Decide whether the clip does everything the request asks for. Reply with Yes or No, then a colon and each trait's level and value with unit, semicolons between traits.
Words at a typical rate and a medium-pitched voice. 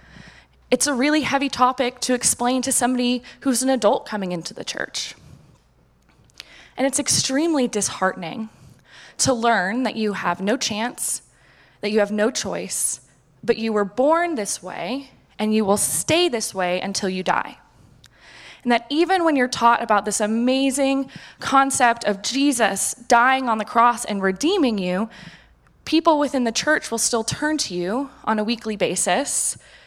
No: average, 160 wpm; high, 235 Hz